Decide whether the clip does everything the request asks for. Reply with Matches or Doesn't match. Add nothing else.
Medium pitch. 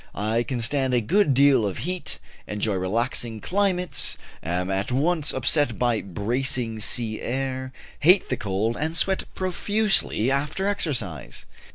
Doesn't match